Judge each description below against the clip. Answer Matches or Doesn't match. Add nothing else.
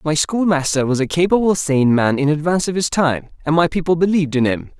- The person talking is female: Doesn't match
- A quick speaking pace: Matches